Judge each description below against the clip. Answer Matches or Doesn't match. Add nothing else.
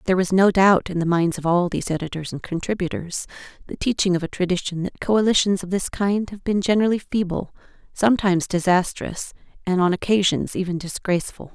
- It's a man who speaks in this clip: Doesn't match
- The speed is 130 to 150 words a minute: Doesn't match